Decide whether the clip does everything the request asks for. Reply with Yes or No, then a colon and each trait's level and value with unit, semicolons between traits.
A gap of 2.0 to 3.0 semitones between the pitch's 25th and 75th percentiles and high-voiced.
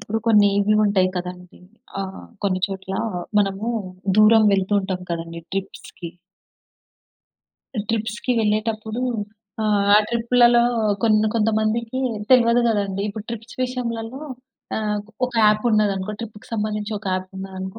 Yes: average, 2.7 semitones; high, 210 Hz